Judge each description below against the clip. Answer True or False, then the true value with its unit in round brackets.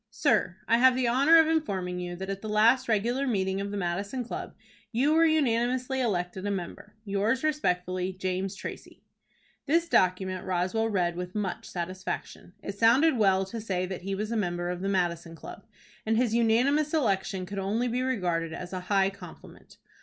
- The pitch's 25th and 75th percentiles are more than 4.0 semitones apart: True (4.7 semitones)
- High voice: True (200 Hz)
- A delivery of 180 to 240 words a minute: True (185 wpm)